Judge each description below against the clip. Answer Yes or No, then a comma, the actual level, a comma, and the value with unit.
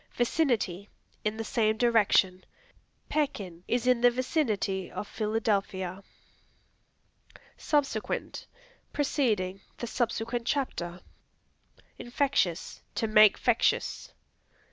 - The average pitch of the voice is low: No, high, 220 Hz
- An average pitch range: Yes, average, 3.9 semitones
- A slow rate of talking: Yes, slow, 85 wpm